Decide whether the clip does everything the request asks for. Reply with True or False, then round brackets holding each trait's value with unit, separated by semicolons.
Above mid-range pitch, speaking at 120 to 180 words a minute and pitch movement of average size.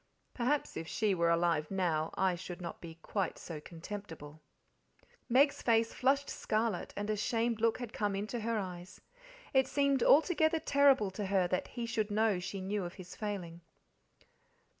True (205 Hz; 165 wpm; 4.7 semitones)